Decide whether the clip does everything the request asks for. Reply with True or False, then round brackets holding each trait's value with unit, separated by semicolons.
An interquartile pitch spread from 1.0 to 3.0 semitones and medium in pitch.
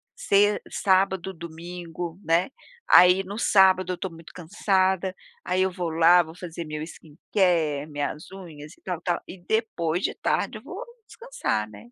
True (2.6 semitones; 180 Hz)